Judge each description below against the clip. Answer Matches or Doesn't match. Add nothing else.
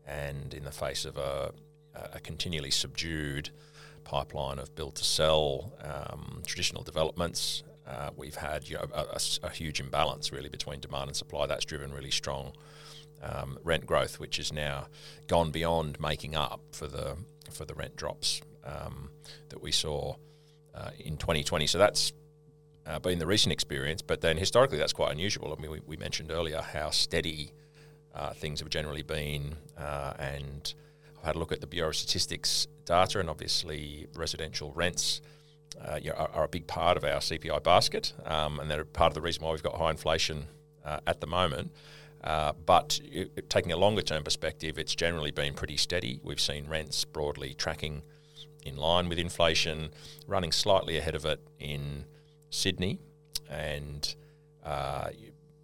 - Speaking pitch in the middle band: Doesn't match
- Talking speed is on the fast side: Doesn't match